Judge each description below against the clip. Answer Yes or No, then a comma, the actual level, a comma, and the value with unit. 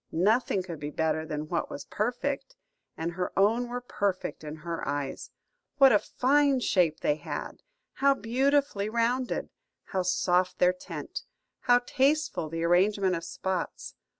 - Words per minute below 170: Yes, average, 150 wpm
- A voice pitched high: Yes, high, 195 Hz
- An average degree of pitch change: No, wide, 6.7 semitones